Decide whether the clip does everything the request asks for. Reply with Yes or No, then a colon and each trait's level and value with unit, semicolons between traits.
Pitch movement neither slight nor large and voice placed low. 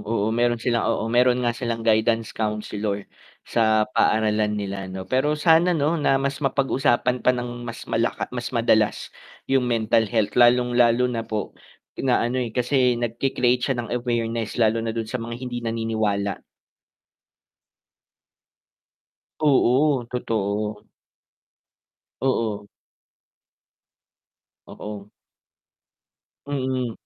No: narrow, 2.3 semitones; low, 115 Hz